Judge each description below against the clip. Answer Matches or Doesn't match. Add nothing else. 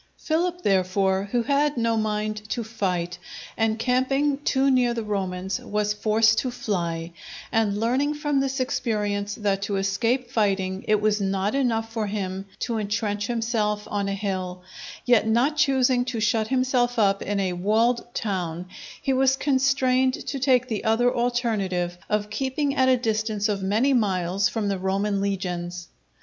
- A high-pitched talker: Matches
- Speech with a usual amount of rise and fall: Matches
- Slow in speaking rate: Doesn't match